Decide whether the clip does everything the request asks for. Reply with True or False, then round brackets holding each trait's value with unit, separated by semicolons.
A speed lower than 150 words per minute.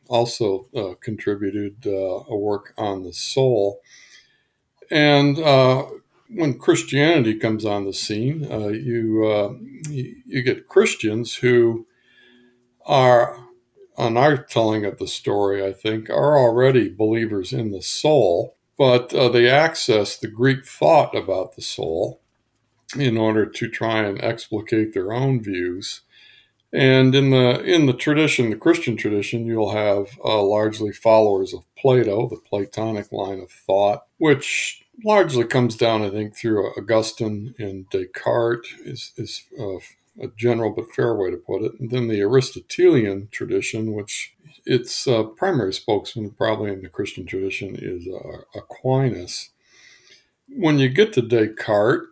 True (140 wpm)